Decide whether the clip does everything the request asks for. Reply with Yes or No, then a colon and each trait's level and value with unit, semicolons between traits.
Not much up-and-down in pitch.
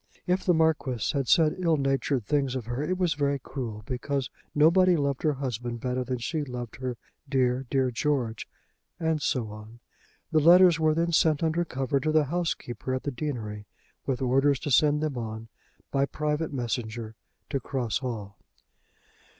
No: average, 4.0 semitones